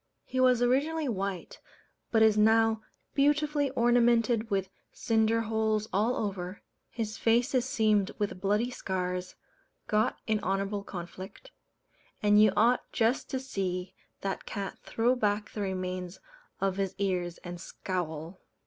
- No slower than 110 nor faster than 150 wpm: Yes, slow, 135 wpm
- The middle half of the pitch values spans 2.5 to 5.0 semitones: Yes, average, 3.6 semitones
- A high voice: Yes, high, 210 Hz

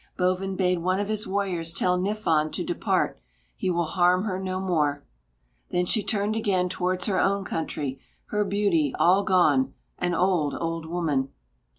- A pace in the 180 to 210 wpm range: No, average, 165 wpm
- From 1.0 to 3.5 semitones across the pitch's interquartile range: Yes, average, 2.9 semitones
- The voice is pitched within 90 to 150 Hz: No, medium, 185 Hz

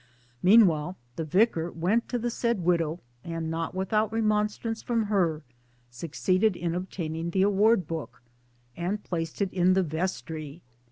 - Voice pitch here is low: No, medium, 180 Hz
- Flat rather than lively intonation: No, average, 4.2 semitones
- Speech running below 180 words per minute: Yes, average, 145 wpm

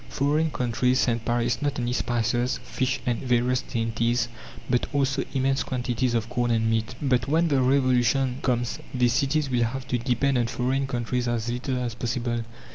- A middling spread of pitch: No, narrow, 1.9 semitones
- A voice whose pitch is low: Yes, low, 125 Hz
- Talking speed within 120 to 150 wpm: No, average, 175 wpm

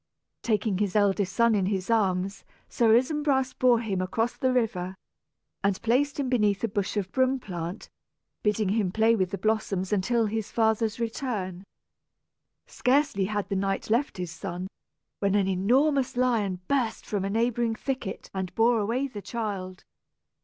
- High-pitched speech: Yes, high, 215 Hz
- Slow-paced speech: No, average, 160 wpm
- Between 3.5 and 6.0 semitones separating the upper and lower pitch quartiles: Yes, average, 3.8 semitones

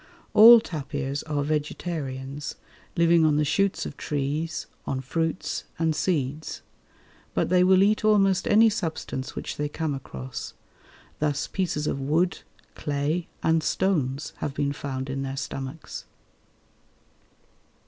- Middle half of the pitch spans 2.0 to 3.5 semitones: No, average, 4.0 semitones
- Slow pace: Yes, slow, 130 wpm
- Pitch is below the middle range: No, medium, 150 Hz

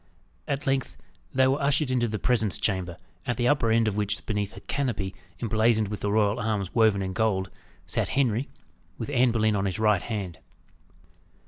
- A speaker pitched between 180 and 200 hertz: No, low, 110 Hz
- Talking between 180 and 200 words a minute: Yes, average, 185 wpm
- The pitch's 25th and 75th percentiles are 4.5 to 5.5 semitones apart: No, average, 3.3 semitones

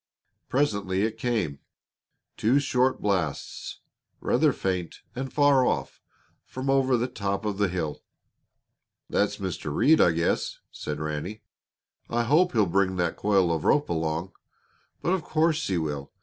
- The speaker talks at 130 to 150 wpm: Yes, average, 145 wpm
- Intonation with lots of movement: Yes, wide, 7.0 semitones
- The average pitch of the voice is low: Yes, low, 100 Hz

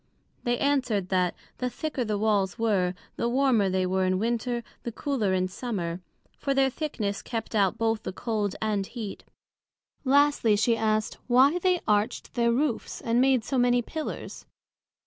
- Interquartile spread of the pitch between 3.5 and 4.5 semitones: Yes, average, 4.1 semitones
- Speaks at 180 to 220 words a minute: No, average, 165 wpm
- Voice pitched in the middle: No, high, 230 Hz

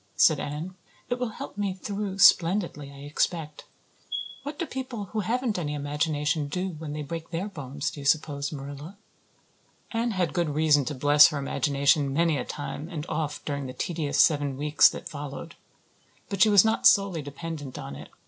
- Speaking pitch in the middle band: Yes, medium, 155 Hz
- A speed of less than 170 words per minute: No, average, 180 wpm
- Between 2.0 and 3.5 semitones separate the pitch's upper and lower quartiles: No, average, 4.5 semitones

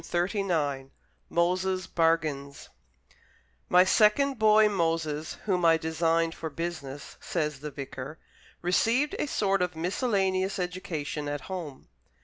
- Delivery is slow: Yes, slow, 115 wpm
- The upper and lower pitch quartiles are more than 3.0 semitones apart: Yes, average, 3.8 semitones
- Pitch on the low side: No, medium, 170 Hz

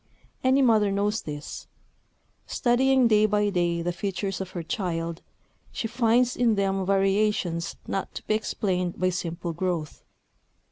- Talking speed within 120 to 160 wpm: Yes, average, 140 wpm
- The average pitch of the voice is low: No, high, 195 Hz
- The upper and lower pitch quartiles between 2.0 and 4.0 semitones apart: Yes, average, 3.7 semitones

